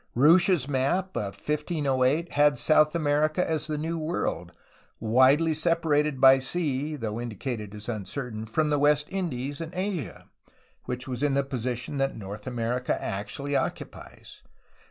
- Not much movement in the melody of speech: No, average, 3.7 semitones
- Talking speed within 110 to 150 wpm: Yes, average, 140 wpm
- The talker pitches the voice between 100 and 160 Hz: Yes, medium, 140 Hz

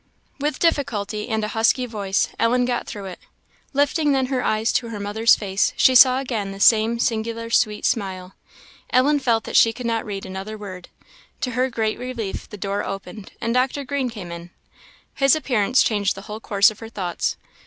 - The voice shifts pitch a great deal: No, average, 3.7 semitones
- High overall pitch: Yes, high, 225 Hz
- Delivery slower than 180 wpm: No, average, 190 wpm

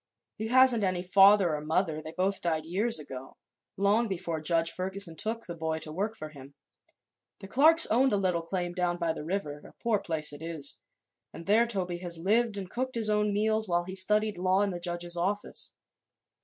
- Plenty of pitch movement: No, average, 4.1 semitones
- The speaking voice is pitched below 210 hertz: Yes, medium, 185 Hz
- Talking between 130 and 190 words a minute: No, average, 200 wpm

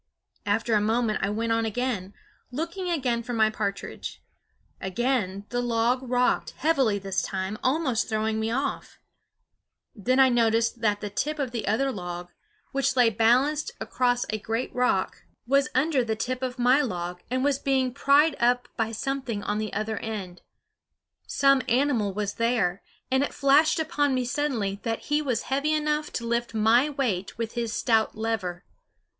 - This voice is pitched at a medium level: No, high, 235 Hz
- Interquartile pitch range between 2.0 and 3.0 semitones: No, average, 3.7 semitones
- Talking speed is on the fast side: No, average, 165 wpm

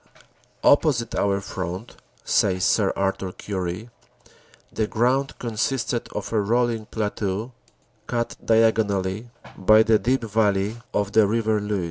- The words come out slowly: Yes, slow, 120 wpm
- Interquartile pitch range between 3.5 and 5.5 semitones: No, average, 2.8 semitones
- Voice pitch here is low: Yes, low, 110 Hz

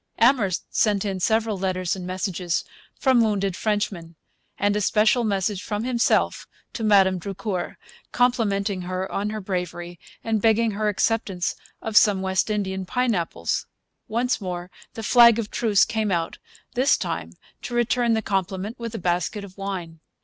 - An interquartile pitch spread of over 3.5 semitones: No, average, 3.2 semitones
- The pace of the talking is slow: No, average, 155 wpm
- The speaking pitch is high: Yes, high, 205 Hz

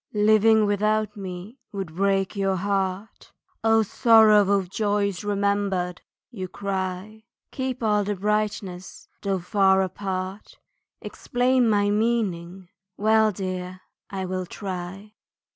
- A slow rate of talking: Yes, slow, 110 wpm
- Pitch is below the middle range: No, high, 200 Hz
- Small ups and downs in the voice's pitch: Yes, narrow, 2.3 semitones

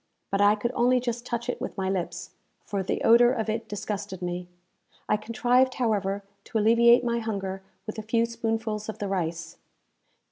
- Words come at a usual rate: Yes, average, 180 wpm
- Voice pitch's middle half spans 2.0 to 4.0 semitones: Yes, average, 3.3 semitones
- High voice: Yes, high, 215 Hz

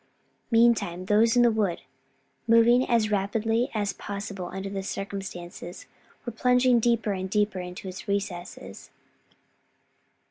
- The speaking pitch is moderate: No, high, 205 Hz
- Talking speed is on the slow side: Yes, slow, 120 wpm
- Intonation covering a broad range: No, average, 3.2 semitones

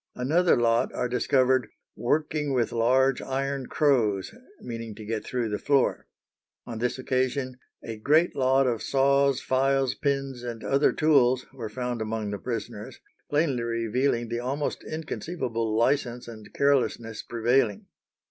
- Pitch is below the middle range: Yes, low, 125 Hz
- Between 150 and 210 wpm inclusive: No, average, 140 wpm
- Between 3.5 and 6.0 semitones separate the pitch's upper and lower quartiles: No, average, 2.9 semitones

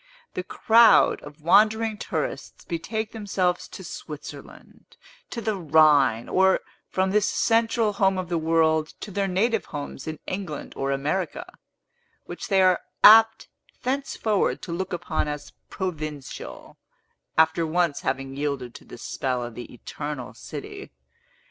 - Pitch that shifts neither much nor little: No, wide, 5.8 semitones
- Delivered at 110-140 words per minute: Yes, slow, 135 wpm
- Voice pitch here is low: No, medium, 175 Hz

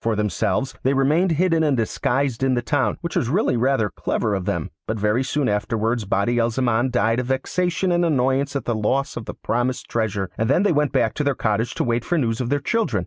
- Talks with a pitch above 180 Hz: No, low, 125 Hz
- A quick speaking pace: Yes, fast, 235 wpm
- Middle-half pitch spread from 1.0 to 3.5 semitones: No, average, 4.0 semitones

